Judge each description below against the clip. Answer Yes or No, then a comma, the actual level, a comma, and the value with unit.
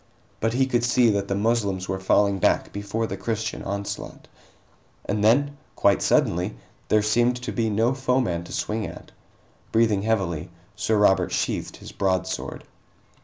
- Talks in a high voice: No, low, 105 Hz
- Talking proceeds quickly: No, average, 155 wpm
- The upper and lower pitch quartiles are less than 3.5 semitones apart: Yes, average, 2.9 semitones